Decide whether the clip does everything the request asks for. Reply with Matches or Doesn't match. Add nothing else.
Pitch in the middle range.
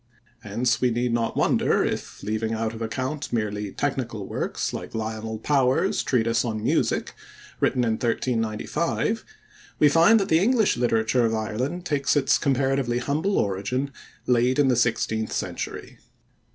Doesn't match